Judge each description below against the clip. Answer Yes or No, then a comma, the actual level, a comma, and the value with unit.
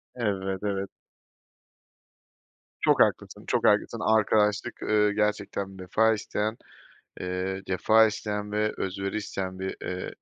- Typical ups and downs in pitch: No, narrow, 1.9 semitones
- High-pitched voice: No, low, 100 Hz